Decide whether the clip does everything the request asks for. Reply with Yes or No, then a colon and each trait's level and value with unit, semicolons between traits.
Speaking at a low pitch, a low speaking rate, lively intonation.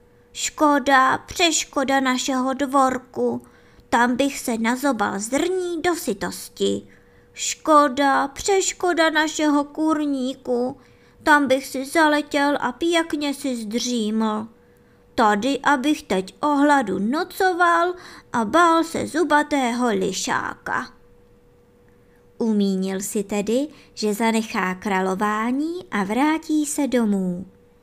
No: very high, 260 Hz; slow, 95 wpm; wide, 6.2 semitones